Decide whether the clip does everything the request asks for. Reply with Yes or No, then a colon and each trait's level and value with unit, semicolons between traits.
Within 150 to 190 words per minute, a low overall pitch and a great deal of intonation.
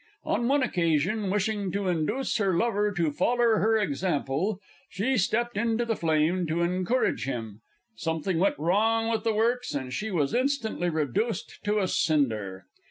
No: average, 160 wpm; high, 195 Hz; wide, 5.9 semitones